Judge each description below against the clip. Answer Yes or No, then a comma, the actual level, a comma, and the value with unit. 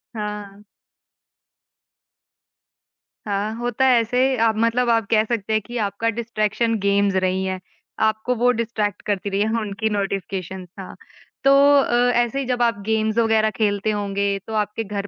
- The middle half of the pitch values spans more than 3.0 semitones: No, narrow, 2.4 semitones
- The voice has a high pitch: Yes, high, 215 Hz